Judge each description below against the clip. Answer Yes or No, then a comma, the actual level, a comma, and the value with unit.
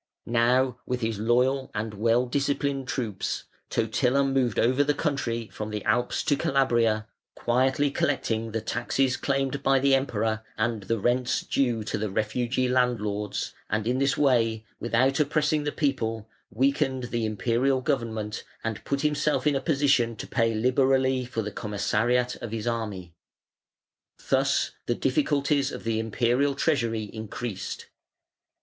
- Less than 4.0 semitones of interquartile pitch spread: Yes, average, 3.3 semitones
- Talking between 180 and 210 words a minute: No, average, 145 wpm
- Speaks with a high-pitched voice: No, low, 120 Hz